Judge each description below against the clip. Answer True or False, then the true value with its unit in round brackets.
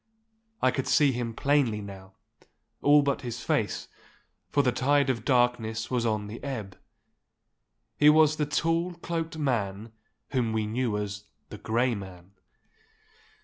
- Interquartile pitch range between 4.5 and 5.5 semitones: True (5.0 semitones)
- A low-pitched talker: True (125 Hz)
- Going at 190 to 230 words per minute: False (140 wpm)